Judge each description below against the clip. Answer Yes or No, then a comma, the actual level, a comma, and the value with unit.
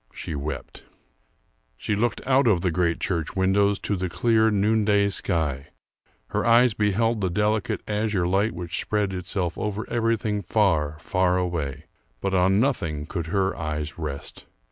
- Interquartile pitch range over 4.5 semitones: No, average, 4.2 semitones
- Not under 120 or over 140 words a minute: No, average, 150 wpm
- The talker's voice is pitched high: No, very low, 95 Hz